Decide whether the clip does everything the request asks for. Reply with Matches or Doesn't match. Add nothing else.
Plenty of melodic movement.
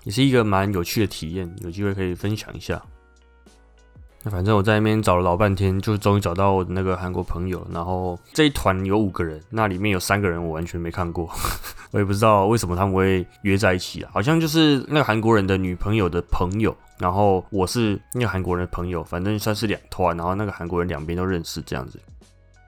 Doesn't match